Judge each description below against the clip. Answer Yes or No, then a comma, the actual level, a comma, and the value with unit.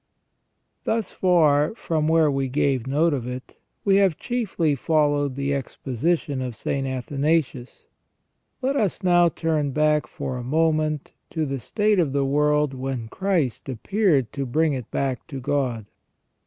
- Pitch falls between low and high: Yes, medium, 145 Hz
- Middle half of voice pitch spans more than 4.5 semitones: No, average, 3.6 semitones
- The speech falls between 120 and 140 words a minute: No, average, 155 wpm